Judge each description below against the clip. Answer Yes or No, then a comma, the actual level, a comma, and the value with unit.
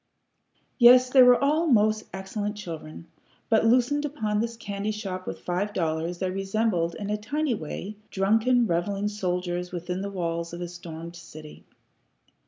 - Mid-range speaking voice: No, high, 200 Hz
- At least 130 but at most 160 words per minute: Yes, average, 155 wpm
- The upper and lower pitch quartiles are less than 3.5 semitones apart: No, average, 4.3 semitones